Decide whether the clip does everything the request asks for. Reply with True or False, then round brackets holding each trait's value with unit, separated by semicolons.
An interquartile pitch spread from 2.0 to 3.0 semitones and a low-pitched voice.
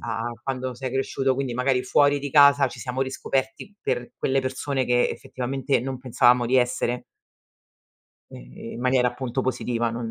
False (1.6 semitones; 130 Hz)